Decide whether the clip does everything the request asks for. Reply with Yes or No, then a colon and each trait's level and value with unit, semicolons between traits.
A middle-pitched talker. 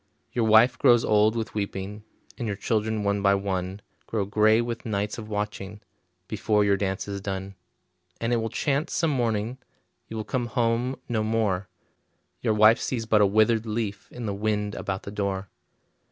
No: low, 105 Hz